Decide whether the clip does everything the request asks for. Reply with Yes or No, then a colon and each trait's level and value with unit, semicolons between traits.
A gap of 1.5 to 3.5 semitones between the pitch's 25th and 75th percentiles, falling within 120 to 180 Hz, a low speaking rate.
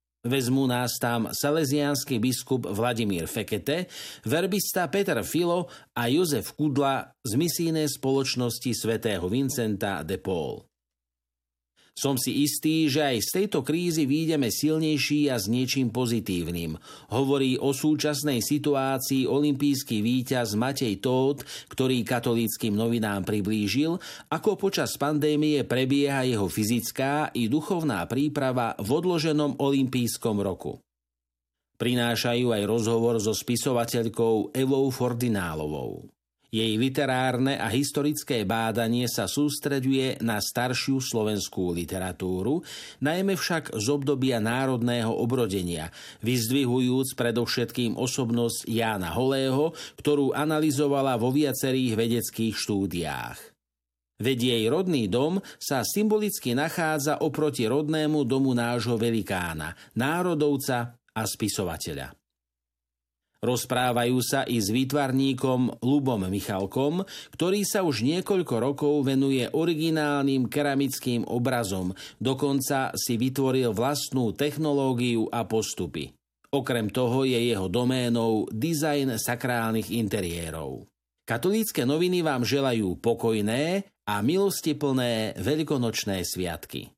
No: average, 4.3 semitones; low, 125 Hz; slow, 105 wpm